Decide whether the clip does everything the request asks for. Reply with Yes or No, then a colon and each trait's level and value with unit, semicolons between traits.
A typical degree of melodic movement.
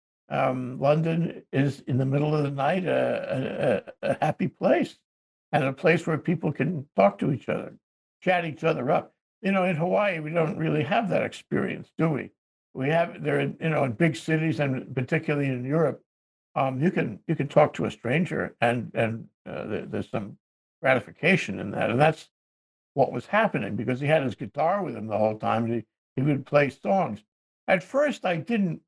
Yes: average, 4.1 semitones